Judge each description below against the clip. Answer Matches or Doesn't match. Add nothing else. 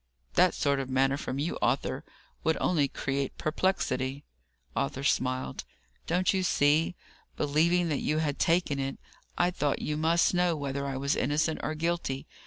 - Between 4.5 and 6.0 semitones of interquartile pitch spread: Doesn't match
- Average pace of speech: Matches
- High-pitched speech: Doesn't match